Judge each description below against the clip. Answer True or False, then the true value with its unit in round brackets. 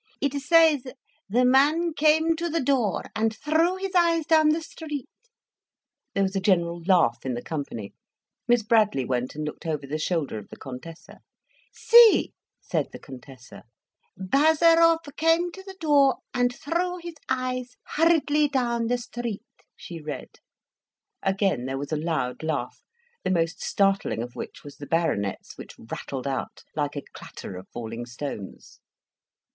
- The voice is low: False (225 Hz)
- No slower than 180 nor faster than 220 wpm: False (155 wpm)